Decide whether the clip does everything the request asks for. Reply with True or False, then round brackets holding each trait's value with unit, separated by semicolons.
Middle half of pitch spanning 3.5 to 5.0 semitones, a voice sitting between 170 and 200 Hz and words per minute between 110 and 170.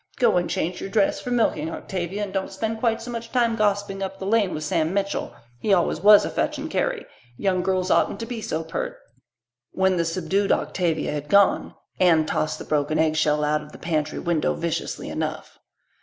False (4.3 semitones; 190 Hz; 200 wpm)